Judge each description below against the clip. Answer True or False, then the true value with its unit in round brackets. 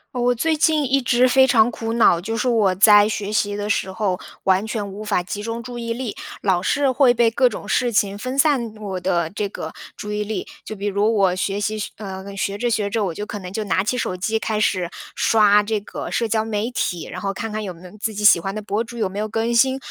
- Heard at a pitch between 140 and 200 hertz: False (215 Hz)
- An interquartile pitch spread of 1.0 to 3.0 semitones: True (2.7 semitones)